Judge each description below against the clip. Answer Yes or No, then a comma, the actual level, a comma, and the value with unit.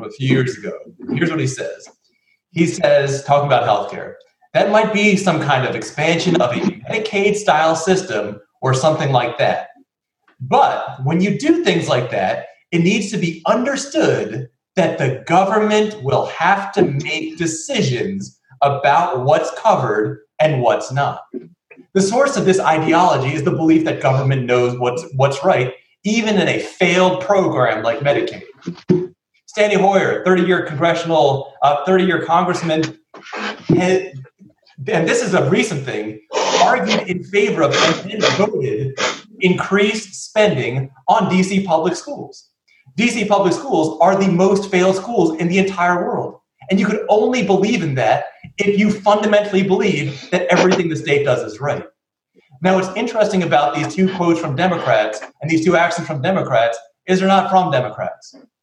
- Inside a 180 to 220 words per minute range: No, average, 155 wpm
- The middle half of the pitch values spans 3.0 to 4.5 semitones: No, average, 5.1 semitones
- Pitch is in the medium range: Yes, medium, 180 Hz